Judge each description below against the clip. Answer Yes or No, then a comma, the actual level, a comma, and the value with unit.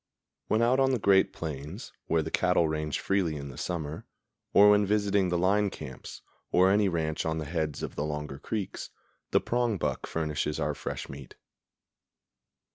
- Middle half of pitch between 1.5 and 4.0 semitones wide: No, average, 4.9 semitones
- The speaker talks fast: No, average, 170 wpm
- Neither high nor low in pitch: No, very low, 85 Hz